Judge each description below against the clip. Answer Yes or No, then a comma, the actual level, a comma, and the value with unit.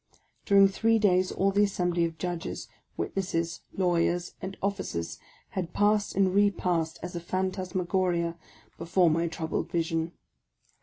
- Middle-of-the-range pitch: Yes, medium, 180 Hz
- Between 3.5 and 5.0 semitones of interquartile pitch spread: No, narrow, 2.4 semitones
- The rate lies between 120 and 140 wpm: Yes, slow, 135 wpm